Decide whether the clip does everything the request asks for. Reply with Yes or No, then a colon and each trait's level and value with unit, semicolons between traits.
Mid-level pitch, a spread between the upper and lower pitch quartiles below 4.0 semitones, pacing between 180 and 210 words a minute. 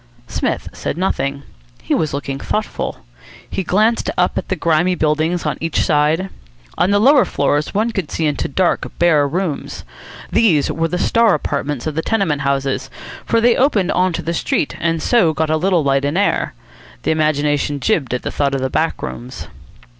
No: medium, 160 Hz; average, 4.6 semitones; average, 185 wpm